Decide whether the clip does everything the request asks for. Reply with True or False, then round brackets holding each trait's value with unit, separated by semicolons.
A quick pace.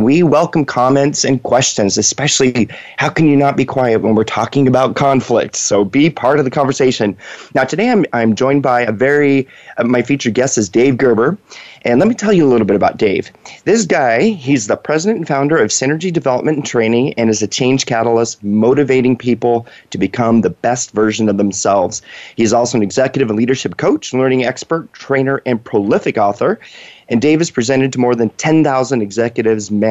False (195 wpm)